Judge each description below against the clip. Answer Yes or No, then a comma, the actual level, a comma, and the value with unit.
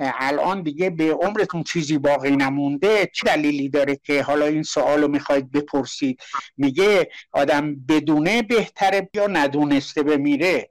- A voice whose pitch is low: No, medium, 150 Hz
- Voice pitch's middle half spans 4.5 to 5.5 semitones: Yes, average, 5.2 semitones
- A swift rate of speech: No, average, 130 wpm